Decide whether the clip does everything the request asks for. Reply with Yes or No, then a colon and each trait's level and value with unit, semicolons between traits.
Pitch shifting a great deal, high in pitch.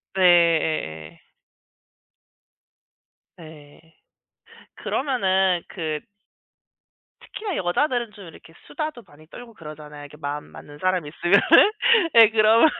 No: wide, 6.8 semitones; medium, 175 Hz